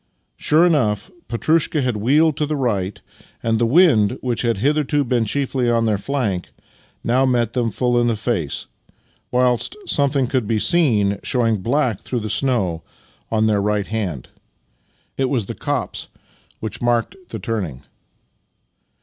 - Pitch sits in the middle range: No, low, 120 Hz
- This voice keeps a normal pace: Yes, average, 150 wpm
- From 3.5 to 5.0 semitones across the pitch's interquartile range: Yes, average, 4.0 semitones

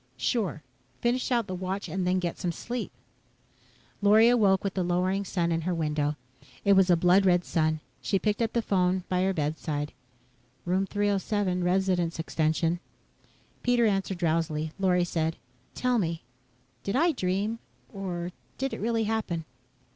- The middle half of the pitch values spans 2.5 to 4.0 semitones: Yes, average, 3.3 semitones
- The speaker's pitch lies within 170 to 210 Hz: Yes, medium, 185 Hz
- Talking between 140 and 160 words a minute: Yes, average, 155 wpm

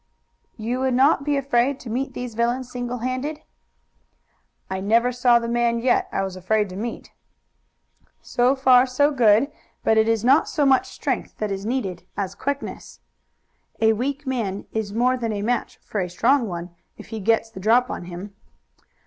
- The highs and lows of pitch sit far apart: No, average, 3.3 semitones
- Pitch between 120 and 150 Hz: No, high, 235 Hz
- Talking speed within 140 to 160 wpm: No, average, 180 wpm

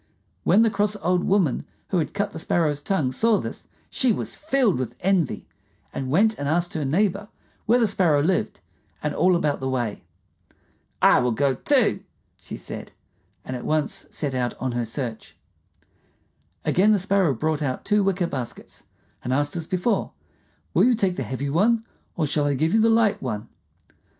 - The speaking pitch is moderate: Yes, medium, 165 Hz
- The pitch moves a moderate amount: No, wide, 6.8 semitones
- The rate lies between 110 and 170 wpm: No, average, 180 wpm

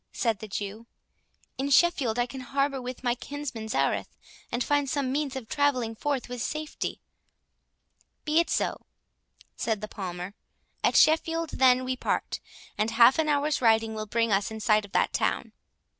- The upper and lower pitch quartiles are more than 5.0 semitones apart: No, average, 4.5 semitones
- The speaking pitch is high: Yes, very high, 250 Hz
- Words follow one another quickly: No, average, 170 wpm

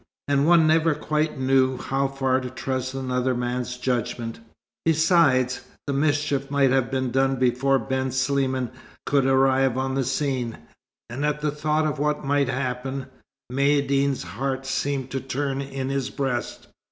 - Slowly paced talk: No, average, 155 wpm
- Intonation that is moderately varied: No, narrow, 1.5 semitones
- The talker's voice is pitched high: No, low, 135 Hz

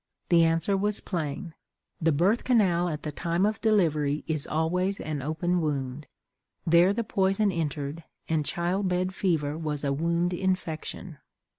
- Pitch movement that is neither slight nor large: Yes, average, 3.5 semitones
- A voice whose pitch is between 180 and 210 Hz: No, medium, 170 Hz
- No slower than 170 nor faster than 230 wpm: No, average, 150 wpm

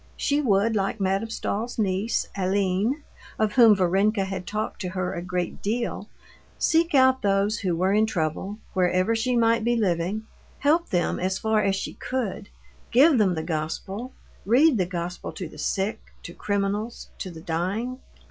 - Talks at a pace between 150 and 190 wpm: Yes, average, 165 wpm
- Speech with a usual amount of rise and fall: Yes, average, 3.7 semitones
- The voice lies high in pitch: Yes, high, 200 Hz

